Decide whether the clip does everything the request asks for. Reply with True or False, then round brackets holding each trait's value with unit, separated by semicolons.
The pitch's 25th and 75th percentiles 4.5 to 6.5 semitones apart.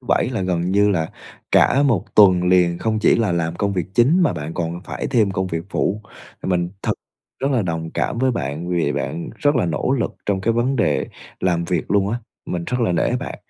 True (5.1 semitones)